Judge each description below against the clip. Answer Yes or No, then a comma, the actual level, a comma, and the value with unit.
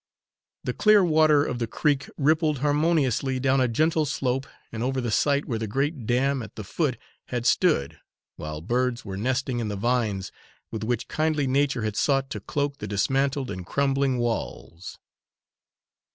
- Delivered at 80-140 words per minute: No, average, 165 wpm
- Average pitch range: Yes, average, 3.8 semitones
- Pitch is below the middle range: Yes, low, 130 Hz